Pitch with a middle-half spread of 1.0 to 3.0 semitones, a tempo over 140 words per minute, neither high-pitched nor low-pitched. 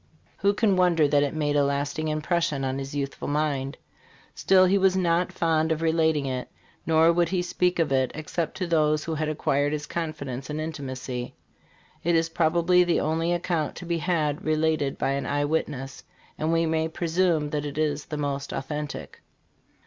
Yes: narrow, 2.6 semitones; average, 185 wpm; medium, 155 Hz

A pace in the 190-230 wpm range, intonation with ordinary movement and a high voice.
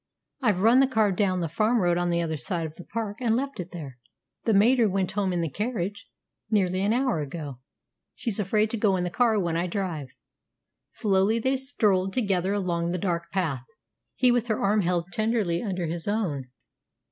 Yes: average, 200 wpm; average, 4.2 semitones; high, 195 Hz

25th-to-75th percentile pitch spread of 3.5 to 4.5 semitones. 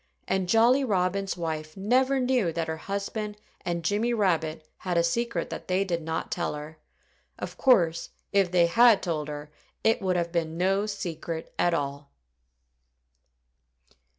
Yes: average, 4.1 semitones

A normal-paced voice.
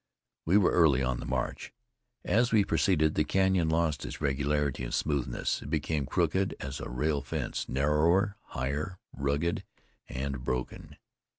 Yes: average, 150 wpm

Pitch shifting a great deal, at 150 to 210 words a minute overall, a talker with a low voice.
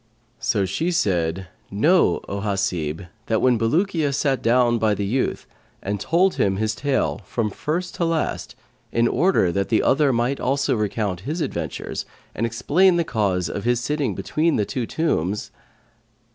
Yes: wide, 6.9 semitones; average, 160 wpm; low, 115 Hz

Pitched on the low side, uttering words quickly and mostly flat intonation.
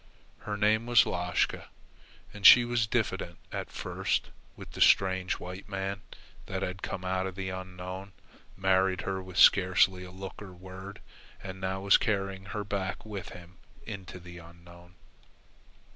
No: very low, 95 Hz; average, 155 wpm; narrow, 1.4 semitones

